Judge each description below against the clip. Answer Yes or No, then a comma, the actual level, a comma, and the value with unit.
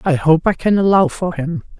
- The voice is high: No, medium, 180 Hz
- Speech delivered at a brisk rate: Yes, fast, 235 wpm